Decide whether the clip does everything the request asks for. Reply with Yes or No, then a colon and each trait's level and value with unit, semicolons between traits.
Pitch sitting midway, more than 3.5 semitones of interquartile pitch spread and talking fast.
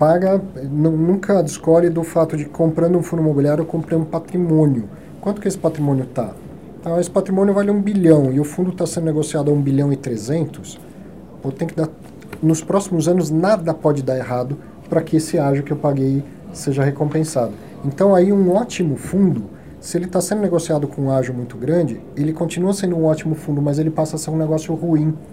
No: medium, 160 Hz; average, 3.2 semitones; fast, 200 wpm